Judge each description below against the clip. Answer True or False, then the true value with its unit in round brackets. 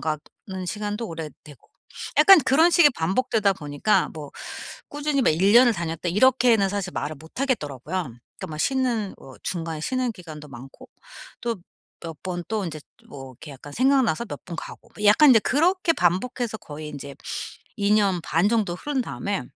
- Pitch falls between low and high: False (195 Hz)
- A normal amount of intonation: False (7.7 semitones)